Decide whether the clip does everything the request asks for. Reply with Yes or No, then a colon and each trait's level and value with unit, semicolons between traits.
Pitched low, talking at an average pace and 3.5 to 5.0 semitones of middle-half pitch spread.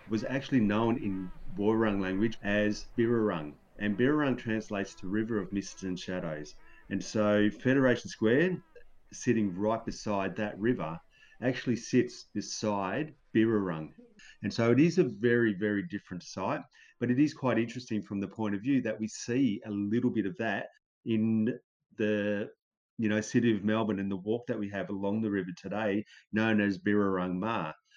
No: low, 105 Hz; average, 165 wpm; narrow, 2.4 semitones